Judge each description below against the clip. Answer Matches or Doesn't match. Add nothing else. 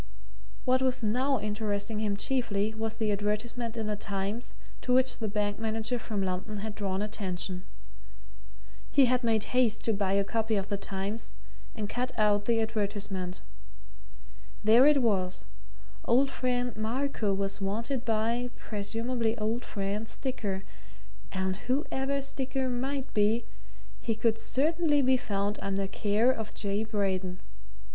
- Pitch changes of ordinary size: Matches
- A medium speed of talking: Matches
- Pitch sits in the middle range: Doesn't match